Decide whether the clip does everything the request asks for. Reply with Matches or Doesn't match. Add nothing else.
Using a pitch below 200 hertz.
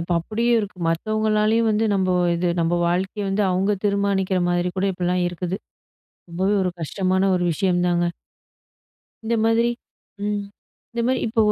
Matches